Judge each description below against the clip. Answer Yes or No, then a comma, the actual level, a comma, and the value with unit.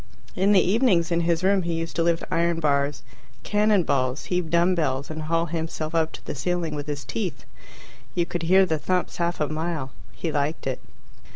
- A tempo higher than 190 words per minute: Yes, average, 200 wpm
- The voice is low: No, medium, 165 Hz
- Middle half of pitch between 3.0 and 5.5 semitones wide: No, narrow, 2.5 semitones